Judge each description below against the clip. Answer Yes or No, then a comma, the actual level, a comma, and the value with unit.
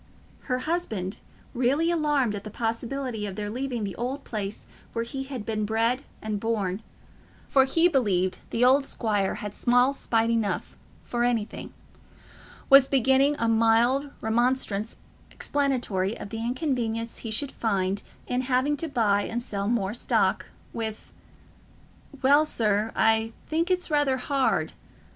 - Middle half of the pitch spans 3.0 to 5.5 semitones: Yes, average, 3.8 semitones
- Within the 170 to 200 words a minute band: No, average, 140 wpm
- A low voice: No, high, 235 Hz